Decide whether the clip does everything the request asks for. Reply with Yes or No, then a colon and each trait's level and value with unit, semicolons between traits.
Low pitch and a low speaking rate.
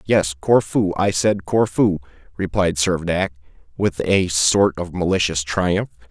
Yes: very low, 90 Hz; slow, 130 wpm